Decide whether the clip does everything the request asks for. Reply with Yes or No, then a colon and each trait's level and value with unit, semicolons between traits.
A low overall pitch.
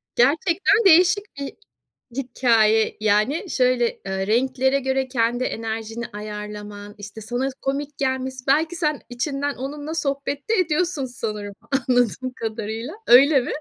No: very high, 255 Hz